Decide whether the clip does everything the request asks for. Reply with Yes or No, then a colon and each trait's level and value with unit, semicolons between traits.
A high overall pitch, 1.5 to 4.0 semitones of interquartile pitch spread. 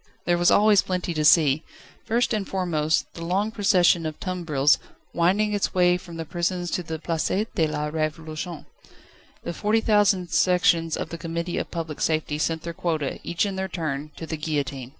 No: medium, 170 Hz; average, 2.8 semitones